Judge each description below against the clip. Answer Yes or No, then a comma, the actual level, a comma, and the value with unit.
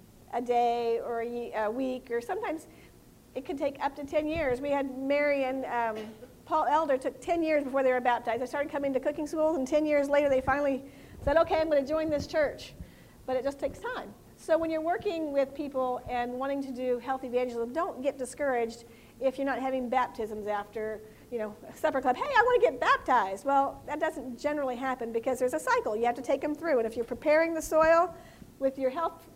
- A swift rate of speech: Yes, fast, 225 wpm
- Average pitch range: Yes, average, 3.7 semitones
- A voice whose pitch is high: Yes, very high, 275 Hz